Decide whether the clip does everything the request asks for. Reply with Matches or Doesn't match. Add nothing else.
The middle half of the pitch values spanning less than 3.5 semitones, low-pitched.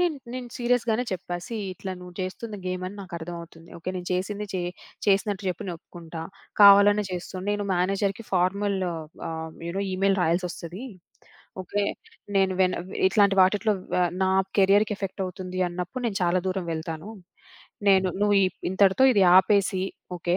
Doesn't match